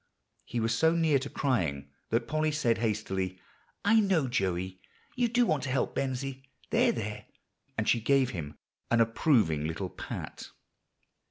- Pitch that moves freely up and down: Yes, wide, 8.0 semitones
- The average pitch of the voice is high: No, low, 120 Hz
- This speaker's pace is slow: No, average, 155 wpm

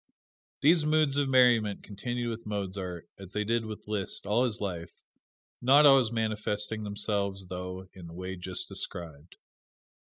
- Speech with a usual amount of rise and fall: Yes, average, 4.2 semitones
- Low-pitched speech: Yes, low, 105 Hz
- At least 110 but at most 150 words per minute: Yes, average, 145 wpm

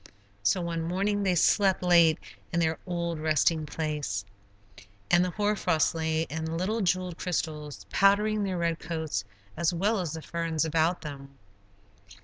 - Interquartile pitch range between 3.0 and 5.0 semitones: No, narrow, 2.5 semitones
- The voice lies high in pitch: No, medium, 170 Hz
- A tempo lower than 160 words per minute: Yes, average, 150 wpm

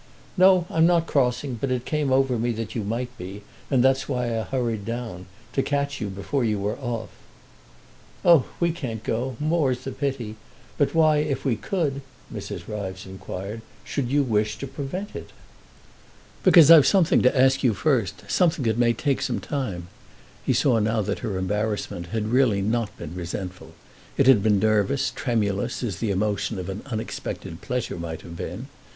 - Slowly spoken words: No, average, 175 wpm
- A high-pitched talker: No, low, 120 Hz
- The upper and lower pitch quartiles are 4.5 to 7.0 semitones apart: Yes, average, 4.8 semitones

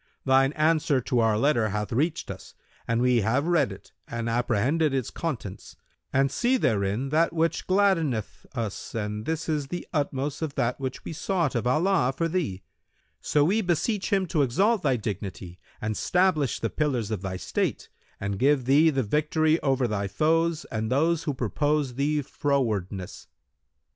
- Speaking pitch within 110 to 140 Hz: Yes, low, 135 Hz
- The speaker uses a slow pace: No, average, 170 wpm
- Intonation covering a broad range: Yes, wide, 5.9 semitones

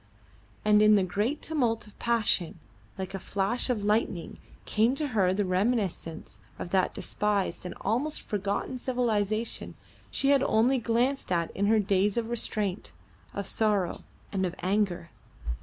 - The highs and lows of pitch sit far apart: No, average, 3.5 semitones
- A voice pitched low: No, high, 210 Hz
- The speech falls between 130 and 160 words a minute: Yes, average, 150 wpm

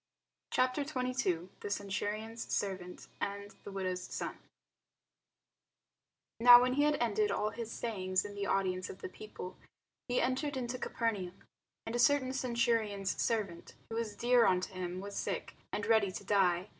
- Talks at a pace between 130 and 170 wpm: Yes, average, 155 wpm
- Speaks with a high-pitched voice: Yes, high, 210 Hz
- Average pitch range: Yes, average, 4.2 semitones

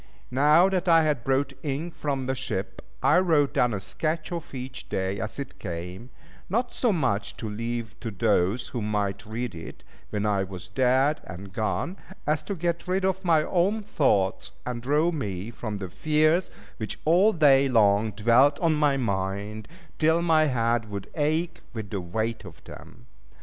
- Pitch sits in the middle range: No, low, 130 Hz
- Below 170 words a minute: No, average, 175 wpm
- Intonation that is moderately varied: No, wide, 7.0 semitones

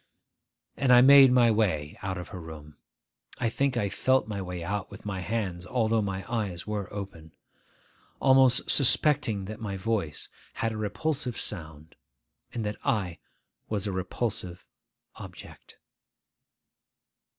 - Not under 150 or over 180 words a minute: No, average, 140 wpm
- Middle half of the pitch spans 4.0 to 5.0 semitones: Yes, average, 4.3 semitones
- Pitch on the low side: Yes, low, 105 Hz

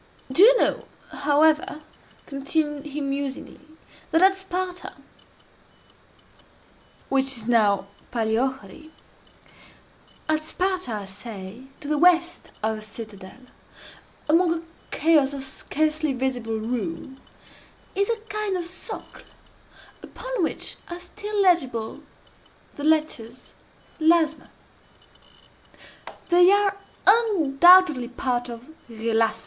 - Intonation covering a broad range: Yes, wide, 6.5 semitones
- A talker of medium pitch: No, very high, 295 Hz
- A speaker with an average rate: No, slow, 100 wpm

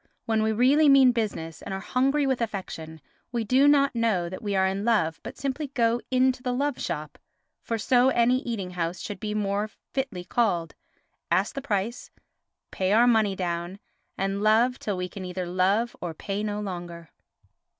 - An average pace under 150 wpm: No, average, 175 wpm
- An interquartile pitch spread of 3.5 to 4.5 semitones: No, average, 5.0 semitones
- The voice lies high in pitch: Yes, high, 210 Hz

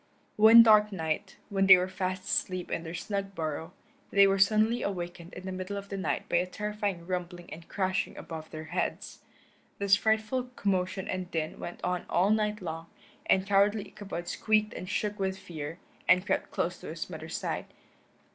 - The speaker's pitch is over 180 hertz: Yes, high, 190 Hz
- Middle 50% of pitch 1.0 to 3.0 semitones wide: Yes, average, 2.7 semitones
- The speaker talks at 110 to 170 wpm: No, average, 185 wpm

